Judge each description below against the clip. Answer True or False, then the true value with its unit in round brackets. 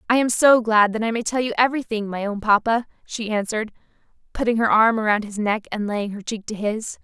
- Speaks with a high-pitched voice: True (220 Hz)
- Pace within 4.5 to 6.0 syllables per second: True (5.9 syllables/s)